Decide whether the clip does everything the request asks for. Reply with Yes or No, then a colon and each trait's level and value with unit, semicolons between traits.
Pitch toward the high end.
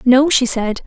Yes: very high, 255 Hz